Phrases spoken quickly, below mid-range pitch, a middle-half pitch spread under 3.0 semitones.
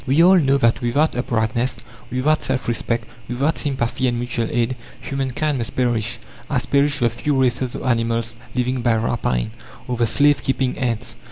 No: average, 175 wpm; low, 125 Hz; narrow, 2.6 semitones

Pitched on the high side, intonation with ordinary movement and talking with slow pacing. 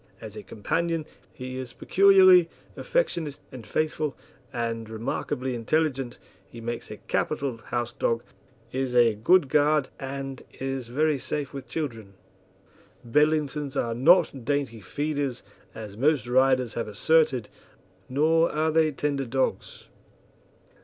No: low, 135 Hz; average, 4.2 semitones; slow, 125 wpm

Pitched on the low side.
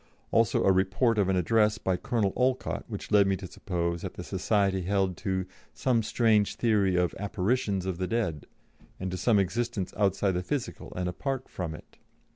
Yes: low, 100 Hz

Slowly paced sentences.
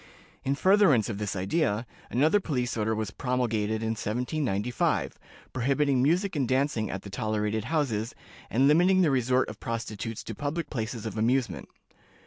No: average, 150 wpm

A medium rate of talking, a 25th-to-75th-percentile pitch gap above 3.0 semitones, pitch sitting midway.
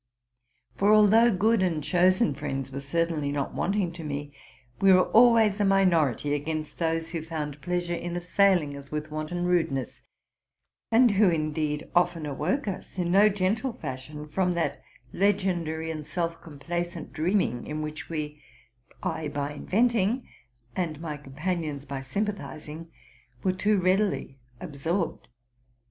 Yes: average, 145 wpm; average, 4.2 semitones; medium, 165 Hz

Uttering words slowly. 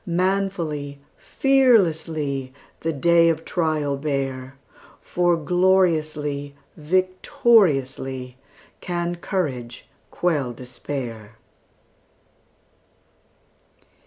Yes: slow, 60 wpm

